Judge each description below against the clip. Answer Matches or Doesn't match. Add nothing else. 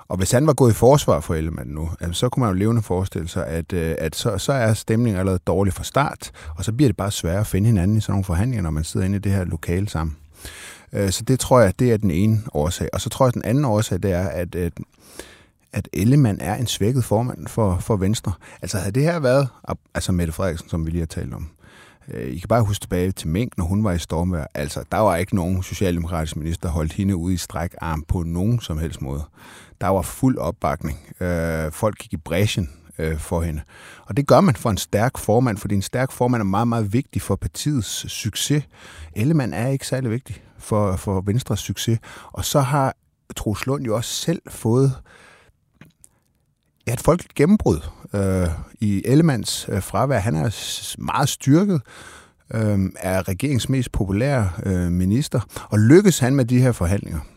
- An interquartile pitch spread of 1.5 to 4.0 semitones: Doesn't match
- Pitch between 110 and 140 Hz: Doesn't match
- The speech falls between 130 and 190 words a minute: Doesn't match